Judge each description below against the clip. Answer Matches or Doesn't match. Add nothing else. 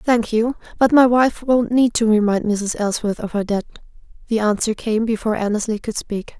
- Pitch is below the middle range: Doesn't match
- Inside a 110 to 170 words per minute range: Doesn't match